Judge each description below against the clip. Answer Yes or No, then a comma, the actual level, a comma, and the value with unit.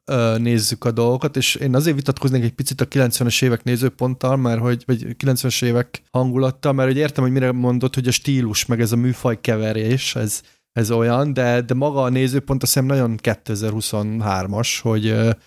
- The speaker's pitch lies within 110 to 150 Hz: Yes, low, 125 Hz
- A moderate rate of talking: No, fast, 180 wpm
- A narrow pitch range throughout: Yes, narrow, 2.1 semitones